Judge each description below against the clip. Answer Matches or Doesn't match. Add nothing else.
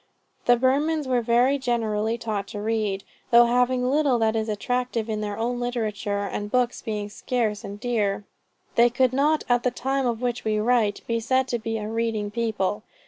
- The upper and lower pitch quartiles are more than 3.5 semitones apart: Doesn't match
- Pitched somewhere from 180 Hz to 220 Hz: Doesn't match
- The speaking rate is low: Doesn't match